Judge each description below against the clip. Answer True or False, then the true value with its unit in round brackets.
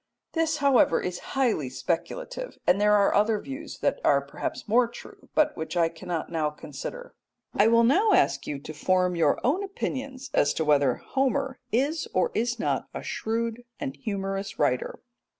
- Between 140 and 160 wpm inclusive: False (170 wpm)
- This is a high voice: True (220 Hz)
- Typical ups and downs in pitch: False (8.2 semitones)